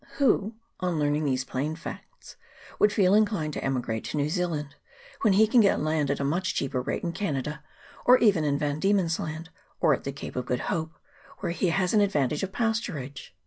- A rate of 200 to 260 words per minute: Yes, fast, 205 wpm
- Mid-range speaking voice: Yes, medium, 160 Hz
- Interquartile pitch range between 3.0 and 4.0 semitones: No, wide, 5.4 semitones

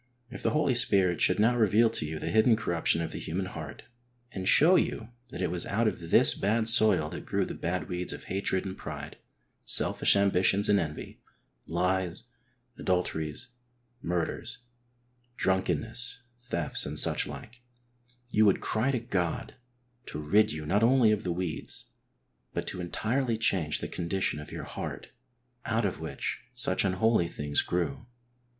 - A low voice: Yes, very low, 95 Hz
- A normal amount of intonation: Yes, average, 4.5 semitones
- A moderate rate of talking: Yes, average, 160 wpm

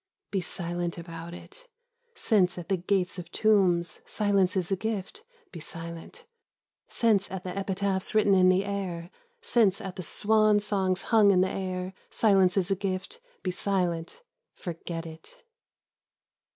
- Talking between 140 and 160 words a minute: Yes, average, 150 wpm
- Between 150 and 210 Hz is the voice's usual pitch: Yes, high, 190 Hz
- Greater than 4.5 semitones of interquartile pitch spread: No, narrow, 2.4 semitones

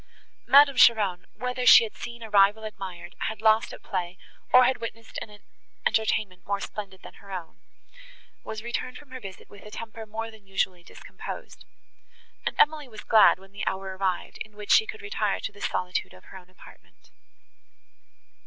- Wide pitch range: No, average, 3.5 semitones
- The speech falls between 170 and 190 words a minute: Yes, average, 180 wpm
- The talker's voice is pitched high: Yes, high, 215 Hz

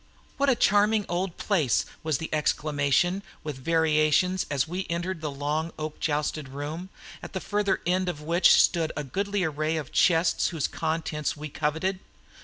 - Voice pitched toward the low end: No, medium, 160 Hz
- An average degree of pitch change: Yes, average, 3.4 semitones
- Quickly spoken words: No, average, 165 wpm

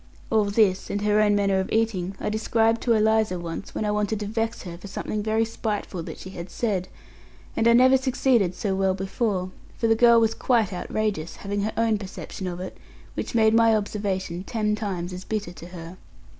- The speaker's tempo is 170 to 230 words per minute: Yes, fast, 205 wpm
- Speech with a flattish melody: No, average, 3.0 semitones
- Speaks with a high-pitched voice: Yes, high, 210 Hz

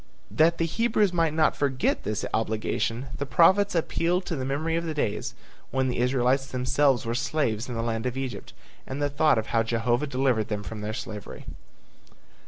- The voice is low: Yes, low, 130 Hz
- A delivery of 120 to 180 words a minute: No, average, 190 wpm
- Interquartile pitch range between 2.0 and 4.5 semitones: No, average, 5.3 semitones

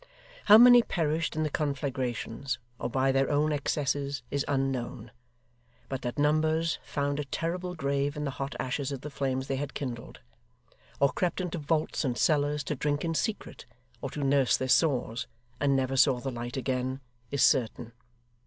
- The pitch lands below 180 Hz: Yes, medium, 140 Hz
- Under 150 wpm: No, average, 170 wpm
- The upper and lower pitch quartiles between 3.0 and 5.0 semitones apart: No, narrow, 2.4 semitones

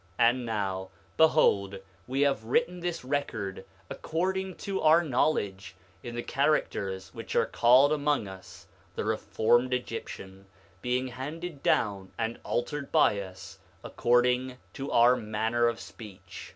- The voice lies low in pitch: Yes, low, 120 Hz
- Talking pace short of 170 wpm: Yes, slow, 135 wpm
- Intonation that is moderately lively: No, wide, 5.8 semitones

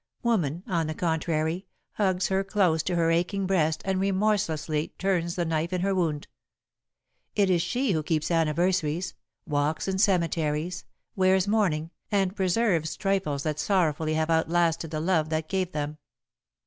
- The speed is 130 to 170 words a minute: Yes, average, 150 wpm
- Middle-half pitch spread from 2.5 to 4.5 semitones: Yes, average, 3.3 semitones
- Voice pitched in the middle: Yes, medium, 170 Hz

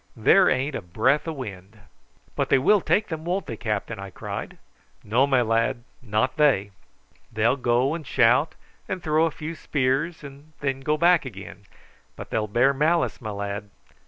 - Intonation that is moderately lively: No, wide, 5.8 semitones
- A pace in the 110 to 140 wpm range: No, average, 175 wpm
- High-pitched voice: No, low, 130 Hz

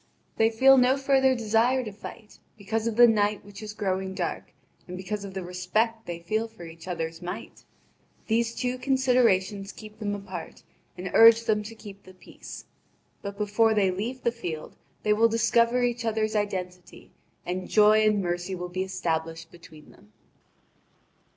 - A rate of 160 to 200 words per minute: Yes, average, 170 wpm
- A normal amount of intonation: Yes, average, 3.7 semitones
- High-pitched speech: Yes, high, 210 Hz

